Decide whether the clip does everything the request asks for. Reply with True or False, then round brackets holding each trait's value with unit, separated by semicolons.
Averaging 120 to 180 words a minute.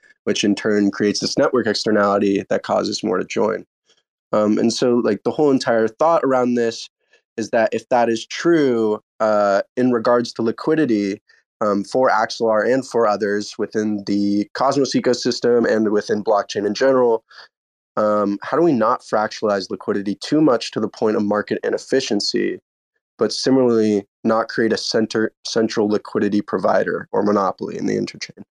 True (160 wpm)